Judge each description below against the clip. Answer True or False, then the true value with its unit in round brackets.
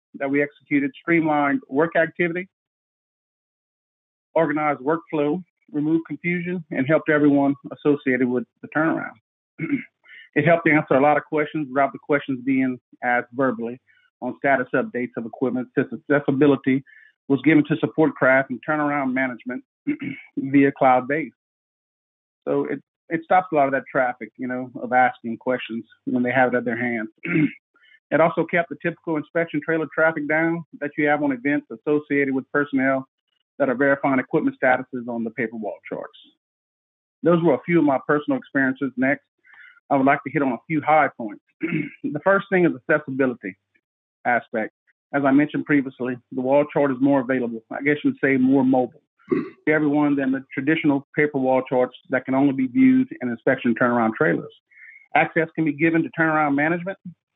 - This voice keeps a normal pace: True (170 wpm)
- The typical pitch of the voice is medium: True (145 Hz)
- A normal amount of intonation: True (3.4 semitones)